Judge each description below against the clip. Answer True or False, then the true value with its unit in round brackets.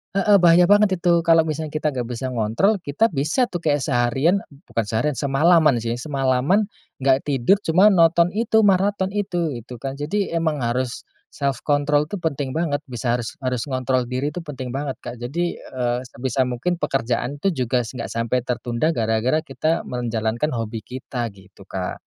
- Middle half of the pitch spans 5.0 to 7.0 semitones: True (5.5 semitones)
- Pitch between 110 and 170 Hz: True (140 Hz)